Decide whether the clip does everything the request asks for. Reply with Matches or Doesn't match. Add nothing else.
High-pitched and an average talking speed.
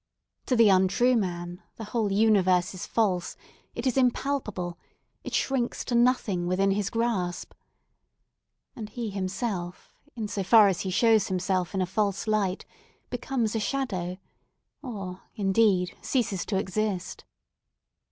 Doesn't match